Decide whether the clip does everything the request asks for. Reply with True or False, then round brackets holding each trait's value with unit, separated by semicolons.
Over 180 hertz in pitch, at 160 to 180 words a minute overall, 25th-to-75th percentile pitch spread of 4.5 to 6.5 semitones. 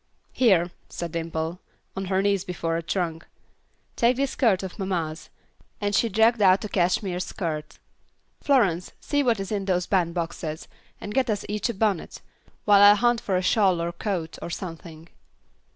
False (190 Hz; 170 wpm; 3.6 semitones)